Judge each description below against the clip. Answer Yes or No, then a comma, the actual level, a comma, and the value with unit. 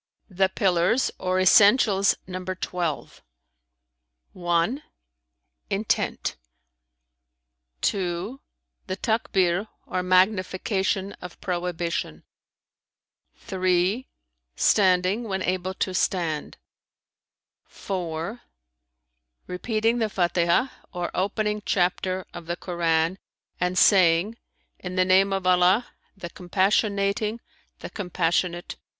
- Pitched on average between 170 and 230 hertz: Yes, medium, 185 Hz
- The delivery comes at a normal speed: No, slow, 85 wpm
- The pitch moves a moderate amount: No, narrow, 2.1 semitones